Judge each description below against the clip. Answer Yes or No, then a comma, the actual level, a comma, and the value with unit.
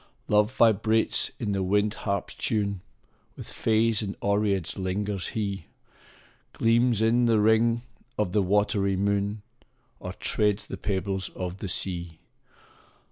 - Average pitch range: No, narrow, 2.1 semitones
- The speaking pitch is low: Yes, low, 105 Hz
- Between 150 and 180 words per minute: No, slow, 135 wpm